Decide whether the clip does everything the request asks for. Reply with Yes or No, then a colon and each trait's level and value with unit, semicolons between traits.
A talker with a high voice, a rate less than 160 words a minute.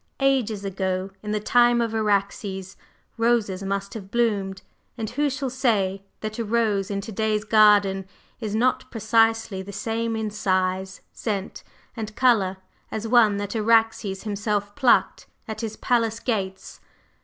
Yes: high, 215 Hz; average, 145 wpm